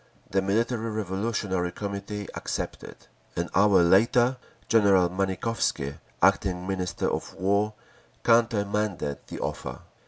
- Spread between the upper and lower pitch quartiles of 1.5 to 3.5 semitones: Yes, average, 2.7 semitones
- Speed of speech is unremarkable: No, slow, 100 wpm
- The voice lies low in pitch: Yes, low, 100 Hz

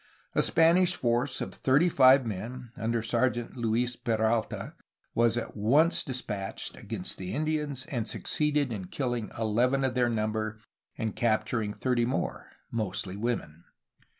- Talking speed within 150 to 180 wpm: No, slow, 135 wpm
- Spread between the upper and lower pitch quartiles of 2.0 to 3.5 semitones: Yes, average, 3.2 semitones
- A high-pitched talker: No, low, 120 Hz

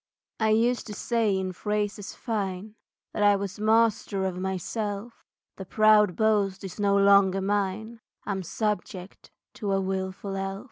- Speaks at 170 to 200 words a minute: No, average, 145 wpm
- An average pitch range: No, narrow, 2.0 semitones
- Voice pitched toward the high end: Yes, high, 200 Hz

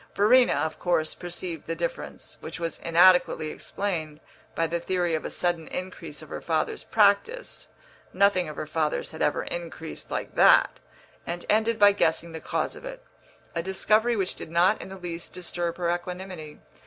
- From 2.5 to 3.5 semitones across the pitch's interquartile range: Yes, average, 2.8 semitones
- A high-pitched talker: No, medium, 175 Hz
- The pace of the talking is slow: No, average, 175 wpm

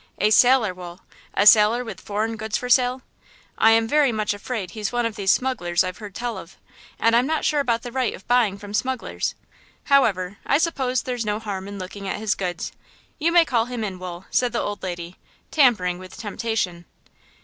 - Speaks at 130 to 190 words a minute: No, average, 200 wpm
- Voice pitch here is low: No, high, 220 Hz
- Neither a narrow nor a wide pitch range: Yes, average, 4.3 semitones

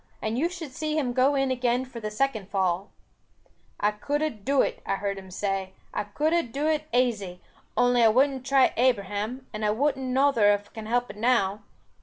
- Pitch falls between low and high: No, high, 245 Hz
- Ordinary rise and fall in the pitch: Yes, average, 4.7 semitones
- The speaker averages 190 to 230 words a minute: Yes, fast, 205 wpm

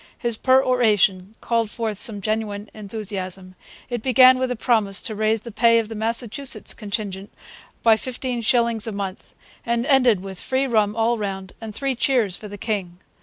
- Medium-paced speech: Yes, average, 170 wpm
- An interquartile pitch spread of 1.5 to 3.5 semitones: Yes, average, 2.8 semitones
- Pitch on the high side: Yes, high, 220 Hz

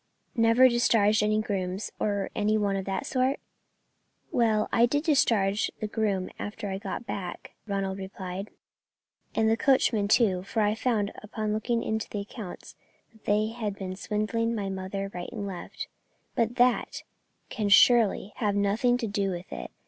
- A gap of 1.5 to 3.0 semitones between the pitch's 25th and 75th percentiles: Yes, narrow, 2.5 semitones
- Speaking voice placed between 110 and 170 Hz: No, high, 210 Hz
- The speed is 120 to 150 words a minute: No, average, 165 wpm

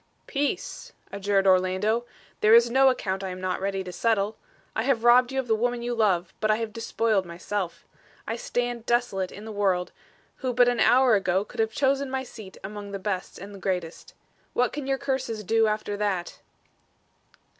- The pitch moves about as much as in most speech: Yes, average, 4.0 semitones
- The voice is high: Yes, high, 215 Hz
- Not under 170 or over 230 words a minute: Yes, average, 190 wpm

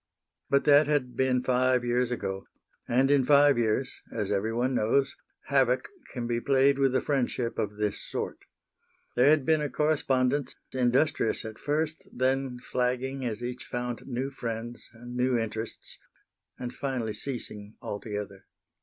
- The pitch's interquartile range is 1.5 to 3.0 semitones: Yes, narrow, 2.5 semitones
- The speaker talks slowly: No, average, 145 wpm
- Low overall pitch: Yes, low, 125 Hz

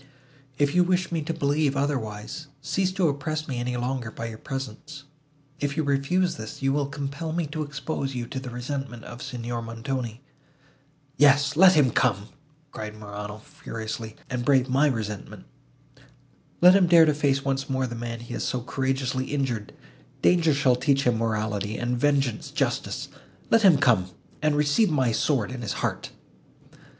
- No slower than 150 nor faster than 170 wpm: Yes, average, 165 wpm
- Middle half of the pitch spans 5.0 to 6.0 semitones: No, average, 3.8 semitones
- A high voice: No, low, 135 Hz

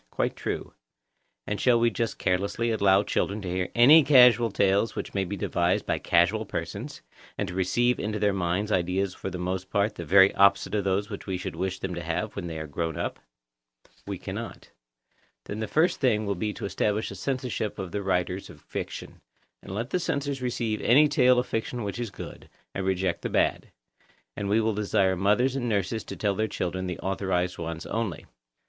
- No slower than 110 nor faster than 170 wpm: No, fast, 205 wpm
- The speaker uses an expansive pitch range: No, average, 3.6 semitones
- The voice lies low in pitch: Yes, low, 100 Hz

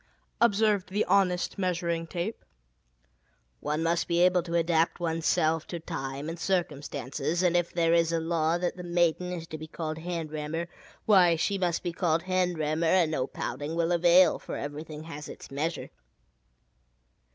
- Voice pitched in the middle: Yes, medium, 170 Hz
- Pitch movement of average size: No, narrow, 2.0 semitones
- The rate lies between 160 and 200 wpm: Yes, average, 175 wpm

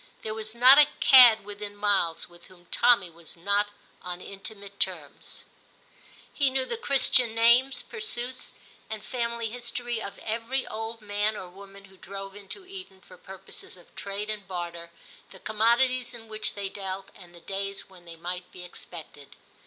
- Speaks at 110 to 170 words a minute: Yes, average, 165 wpm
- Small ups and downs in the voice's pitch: No, average, 3.8 semitones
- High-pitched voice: Yes, high, 205 Hz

